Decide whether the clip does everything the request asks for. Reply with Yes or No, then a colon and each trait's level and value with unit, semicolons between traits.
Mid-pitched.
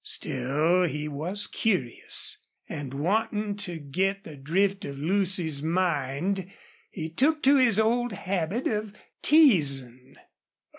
Yes: medium, 180 Hz